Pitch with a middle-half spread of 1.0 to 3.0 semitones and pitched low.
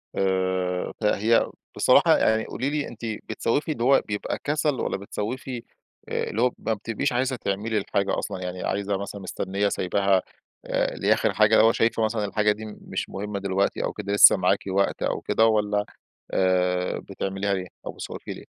Yes: average, 2.7 semitones; low, 105 Hz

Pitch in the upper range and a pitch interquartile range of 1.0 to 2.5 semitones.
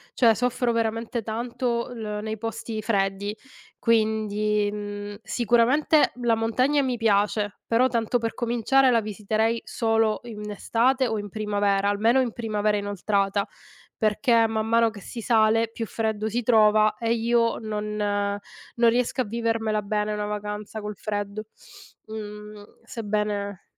Yes: high, 220 Hz; narrow, 1.8 semitones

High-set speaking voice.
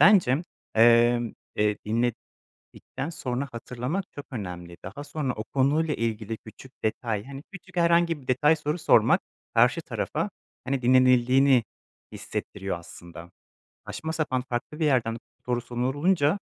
No: low, 130 Hz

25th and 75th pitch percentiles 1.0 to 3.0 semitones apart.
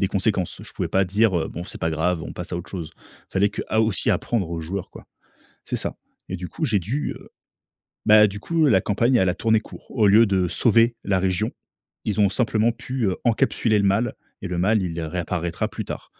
No: average, 3.7 semitones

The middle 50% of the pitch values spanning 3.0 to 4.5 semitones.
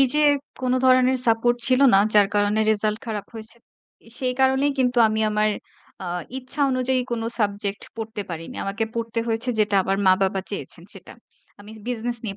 Yes: average, 3.6 semitones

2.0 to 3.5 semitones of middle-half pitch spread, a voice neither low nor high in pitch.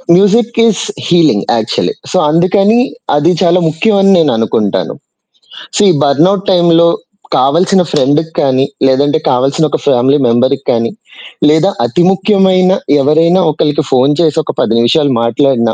No: wide, 5.4 semitones; medium, 155 Hz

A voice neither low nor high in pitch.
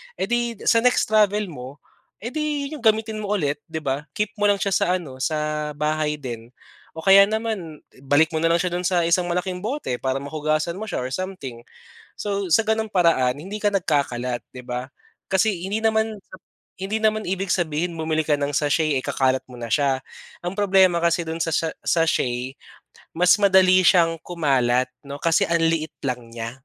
Yes: medium, 165 Hz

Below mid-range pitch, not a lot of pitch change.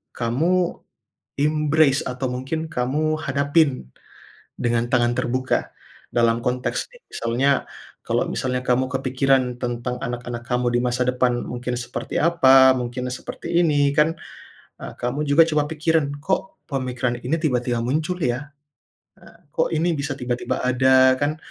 No: low, 130 Hz; average, 3.4 semitones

